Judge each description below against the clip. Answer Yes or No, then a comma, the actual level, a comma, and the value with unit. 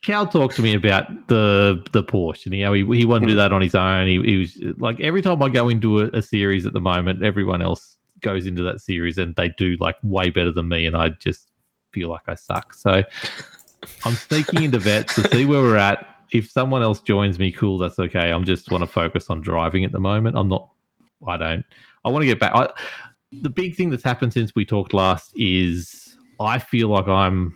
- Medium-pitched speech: No, low, 100 Hz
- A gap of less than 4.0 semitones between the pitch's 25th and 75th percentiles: No, average, 4.3 semitones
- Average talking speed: No, fast, 235 wpm